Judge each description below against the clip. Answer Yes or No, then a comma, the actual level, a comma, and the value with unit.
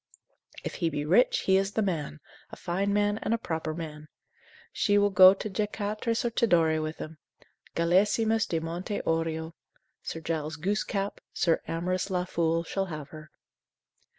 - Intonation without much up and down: No, average, 4.0 semitones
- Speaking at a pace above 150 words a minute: Yes, average, 160 wpm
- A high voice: No, medium, 175 Hz